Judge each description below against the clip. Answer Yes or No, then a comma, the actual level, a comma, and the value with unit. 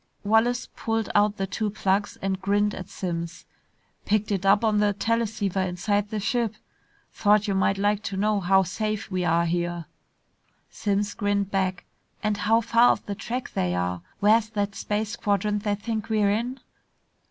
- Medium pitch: No, high, 205 Hz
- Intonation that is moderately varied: No, narrow, 1.8 semitones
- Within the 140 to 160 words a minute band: No, average, 175 wpm